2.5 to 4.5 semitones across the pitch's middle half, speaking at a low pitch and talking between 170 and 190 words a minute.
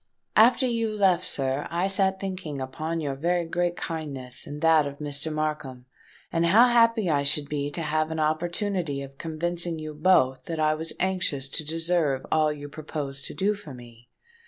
No: average, 3.6 semitones; medium, 155 Hz; average, 180 wpm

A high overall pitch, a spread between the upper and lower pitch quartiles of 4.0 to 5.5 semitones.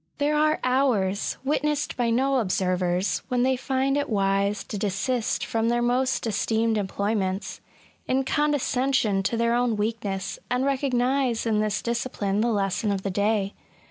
Yes: high, 230 Hz; average, 4.5 semitones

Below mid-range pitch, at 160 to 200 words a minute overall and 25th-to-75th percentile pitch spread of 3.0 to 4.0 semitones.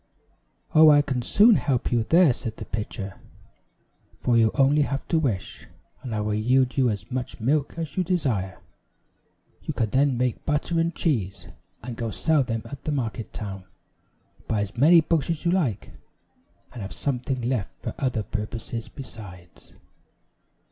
No: low, 125 Hz; average, 165 wpm; average, 5.0 semitones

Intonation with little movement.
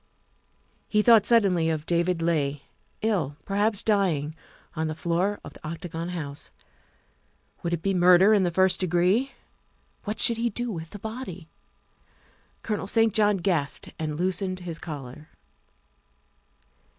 No: average, 4.2 semitones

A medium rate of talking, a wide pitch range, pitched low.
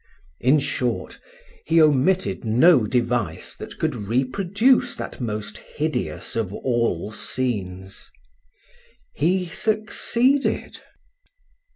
No: slow, 85 wpm; wide, 8.5 semitones; low, 130 Hz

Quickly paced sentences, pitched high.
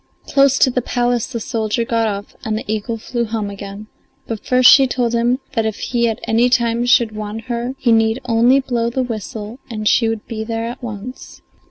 Yes: fast, 210 wpm; high, 230 Hz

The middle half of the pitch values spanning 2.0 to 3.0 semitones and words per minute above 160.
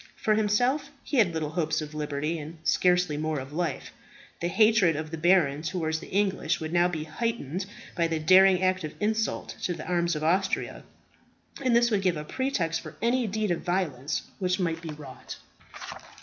No: average, 3.9 semitones; average, 190 wpm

